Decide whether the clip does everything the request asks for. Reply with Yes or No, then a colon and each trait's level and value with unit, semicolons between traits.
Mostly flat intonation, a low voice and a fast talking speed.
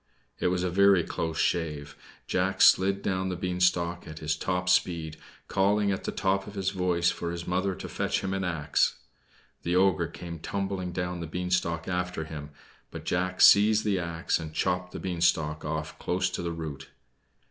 No: narrow, 2.2 semitones; very low, 90 Hz; average, 180 wpm